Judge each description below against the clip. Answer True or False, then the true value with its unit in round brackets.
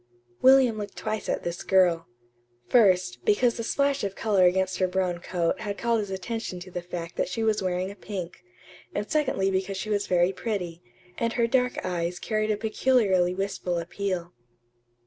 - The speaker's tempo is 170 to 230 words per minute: True (180 wpm)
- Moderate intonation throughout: True (3.4 semitones)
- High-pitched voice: True (195 Hz)